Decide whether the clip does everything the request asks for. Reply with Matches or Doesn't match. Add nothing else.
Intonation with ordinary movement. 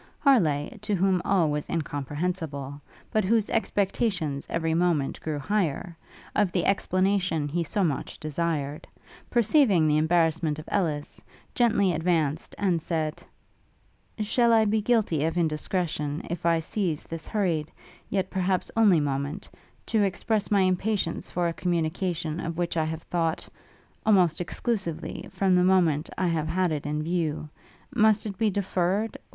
Matches